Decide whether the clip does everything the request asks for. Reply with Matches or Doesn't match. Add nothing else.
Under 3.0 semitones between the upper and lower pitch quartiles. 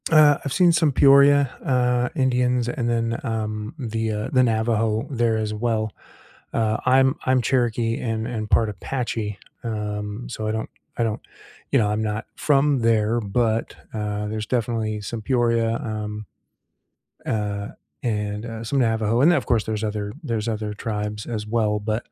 Matches